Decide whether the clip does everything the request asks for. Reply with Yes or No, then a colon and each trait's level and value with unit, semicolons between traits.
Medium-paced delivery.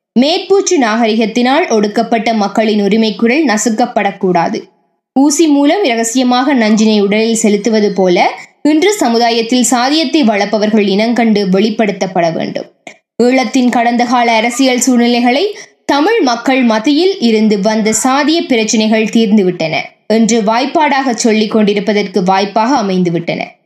Yes: average, 100 wpm